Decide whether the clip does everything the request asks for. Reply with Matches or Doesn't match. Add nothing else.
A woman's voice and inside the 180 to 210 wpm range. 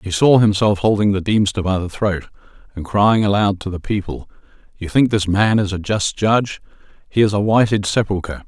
Doesn't match